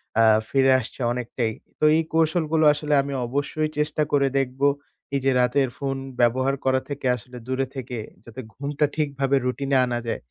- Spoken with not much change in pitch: Yes, narrow, 2.3 semitones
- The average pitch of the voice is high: No, low, 135 Hz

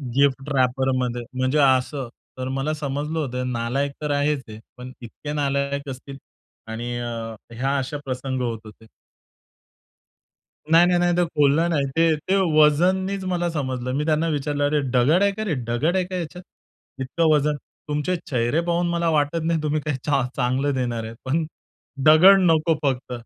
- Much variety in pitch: No, average, 3.8 semitones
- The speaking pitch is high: No, medium, 145 Hz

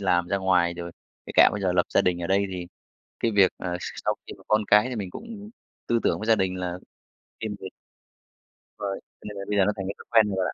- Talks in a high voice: No, very low, 95 Hz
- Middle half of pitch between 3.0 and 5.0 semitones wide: No, narrow, 2.6 semitones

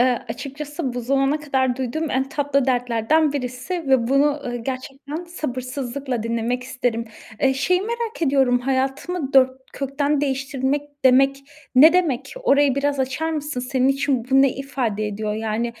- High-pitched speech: Yes, very high, 270 Hz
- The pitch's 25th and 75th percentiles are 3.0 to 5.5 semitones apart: No, narrow, 2.5 semitones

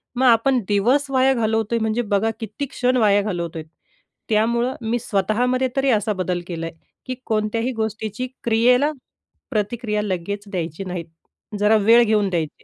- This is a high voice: Yes, high, 220 Hz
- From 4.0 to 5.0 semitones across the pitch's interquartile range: No, average, 3.2 semitones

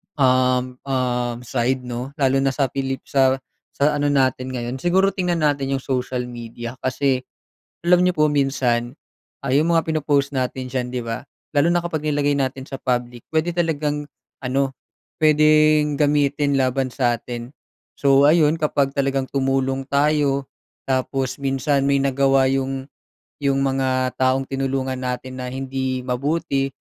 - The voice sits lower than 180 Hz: Yes, low, 135 Hz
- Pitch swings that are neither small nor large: No, narrow, 2.1 semitones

